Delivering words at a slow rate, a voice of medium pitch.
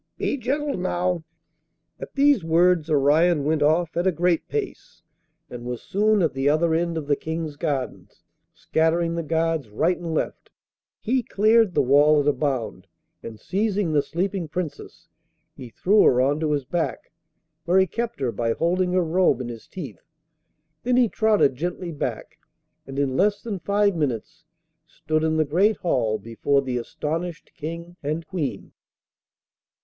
No: average, 165 wpm; medium, 165 Hz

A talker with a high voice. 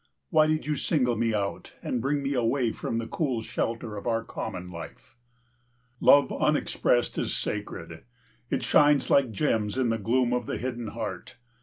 No: low, 120 Hz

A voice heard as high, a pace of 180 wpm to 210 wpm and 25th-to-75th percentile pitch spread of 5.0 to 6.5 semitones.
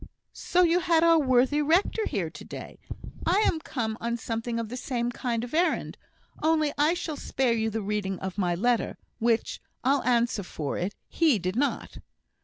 Yes: high, 245 Hz; average, 185 wpm; wide, 5.6 semitones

